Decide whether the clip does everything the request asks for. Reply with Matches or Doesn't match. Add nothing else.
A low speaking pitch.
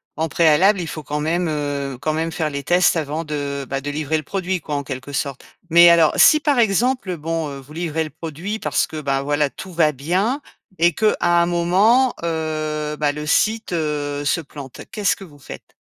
Doesn't match